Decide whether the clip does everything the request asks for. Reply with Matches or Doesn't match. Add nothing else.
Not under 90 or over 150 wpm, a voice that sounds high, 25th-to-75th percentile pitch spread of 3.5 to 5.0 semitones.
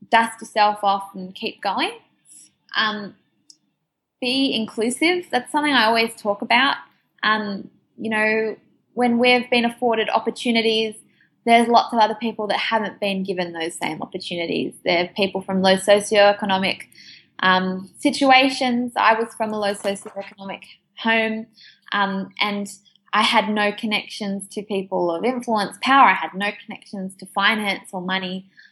Doesn't match